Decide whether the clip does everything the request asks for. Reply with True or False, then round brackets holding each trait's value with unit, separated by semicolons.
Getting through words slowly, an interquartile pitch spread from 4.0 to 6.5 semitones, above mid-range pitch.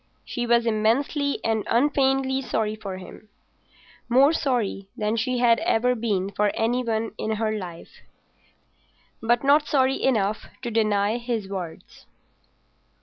False (130 wpm; 3.0 semitones; 230 Hz)